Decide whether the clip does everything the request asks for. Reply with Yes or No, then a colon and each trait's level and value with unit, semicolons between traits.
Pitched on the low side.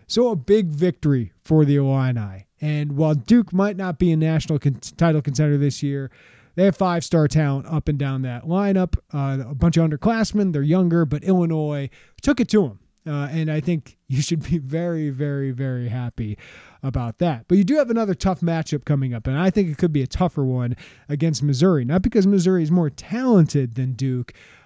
No: medium, 155 Hz